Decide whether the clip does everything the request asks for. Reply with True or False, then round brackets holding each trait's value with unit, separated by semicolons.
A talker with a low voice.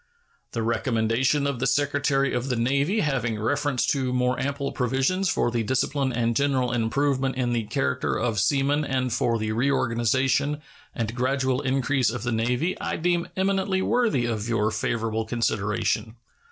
True (130 Hz)